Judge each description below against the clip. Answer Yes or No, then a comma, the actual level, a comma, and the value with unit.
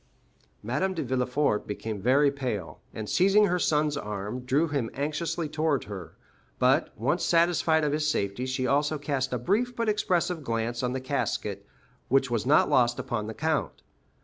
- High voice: No, medium, 140 Hz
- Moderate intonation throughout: Yes, average, 4.8 semitones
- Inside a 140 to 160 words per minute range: No, average, 170 wpm